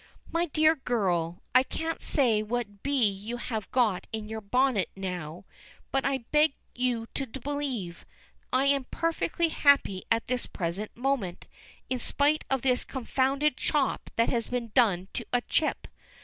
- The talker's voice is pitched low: No, high, 245 Hz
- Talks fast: No, average, 155 wpm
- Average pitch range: Yes, average, 4.6 semitones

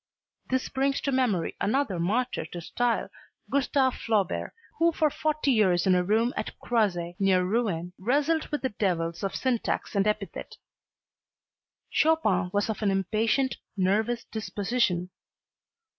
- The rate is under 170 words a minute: Yes, slow, 135 wpm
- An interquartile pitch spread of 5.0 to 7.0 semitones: Yes, wide, 5.6 semitones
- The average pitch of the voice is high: Yes, high, 215 Hz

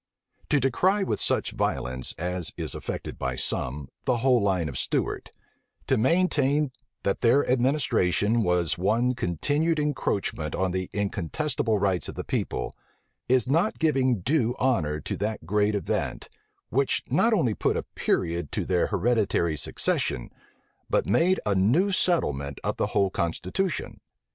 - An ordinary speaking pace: Yes, average, 145 wpm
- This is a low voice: Yes, low, 110 Hz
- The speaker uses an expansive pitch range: Yes, wide, 7.7 semitones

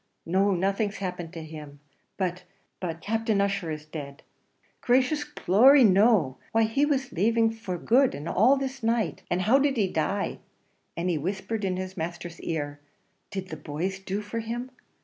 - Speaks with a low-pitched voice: No, high, 195 Hz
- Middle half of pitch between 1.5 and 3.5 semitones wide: No, average, 5.1 semitones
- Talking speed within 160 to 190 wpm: Yes, average, 170 wpm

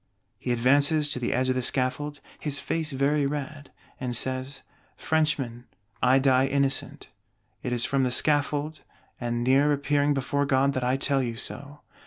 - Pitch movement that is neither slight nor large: No, narrow, 2.1 semitones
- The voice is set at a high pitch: No, medium, 140 Hz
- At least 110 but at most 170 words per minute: Yes, average, 165 wpm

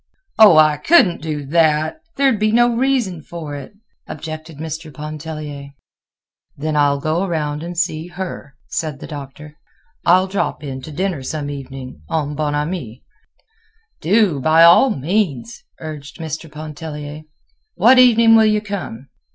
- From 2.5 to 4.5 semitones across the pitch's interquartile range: Yes, average, 4.0 semitones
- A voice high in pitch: No, medium, 155 Hz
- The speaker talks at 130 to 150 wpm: Yes, average, 145 wpm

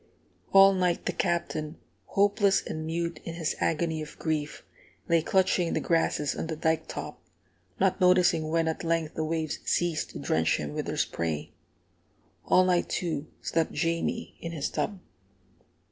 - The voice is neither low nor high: Yes, medium, 165 Hz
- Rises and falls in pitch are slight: Yes, narrow, 2.1 semitones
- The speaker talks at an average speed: Yes, average, 160 wpm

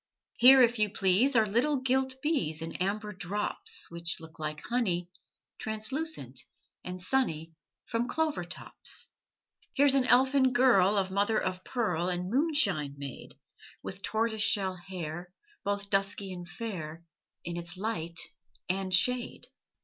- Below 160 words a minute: Yes, slow, 135 wpm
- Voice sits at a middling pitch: No, high, 200 Hz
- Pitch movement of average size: No, wide, 5.7 semitones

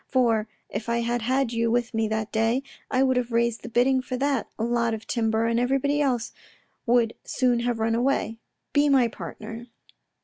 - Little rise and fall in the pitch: Yes, narrow, 2.0 semitones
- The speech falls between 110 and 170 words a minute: No, average, 190 wpm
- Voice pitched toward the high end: Yes, high, 235 Hz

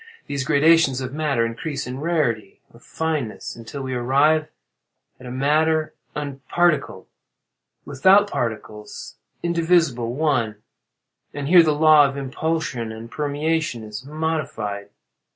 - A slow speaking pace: Yes, slow, 105 wpm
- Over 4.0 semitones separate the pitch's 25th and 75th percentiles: Yes, average, 4.7 semitones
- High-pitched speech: No, medium, 140 Hz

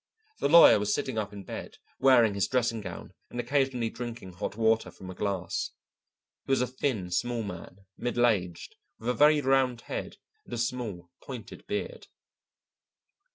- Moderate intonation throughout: Yes, average, 4.0 semitones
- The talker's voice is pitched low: Yes, low, 115 Hz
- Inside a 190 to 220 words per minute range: No, average, 165 wpm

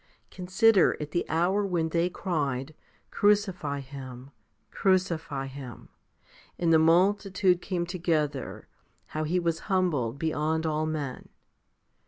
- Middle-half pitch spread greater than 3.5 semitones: Yes, average, 4.0 semitones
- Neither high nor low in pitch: Yes, medium, 165 Hz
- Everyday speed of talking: No, slow, 120 wpm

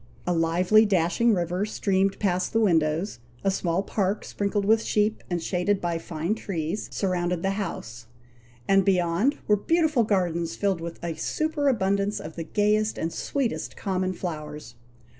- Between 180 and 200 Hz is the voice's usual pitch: Yes, high, 190 Hz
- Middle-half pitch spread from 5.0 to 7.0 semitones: No, average, 3.7 semitones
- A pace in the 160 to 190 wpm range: No, average, 150 wpm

